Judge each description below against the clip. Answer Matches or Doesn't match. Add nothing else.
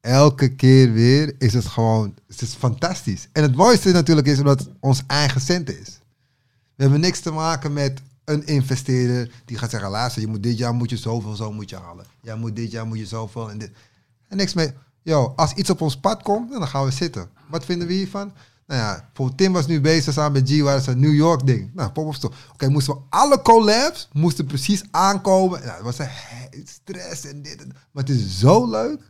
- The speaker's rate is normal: Doesn't match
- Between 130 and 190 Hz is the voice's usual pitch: Matches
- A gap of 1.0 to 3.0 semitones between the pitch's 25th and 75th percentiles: Doesn't match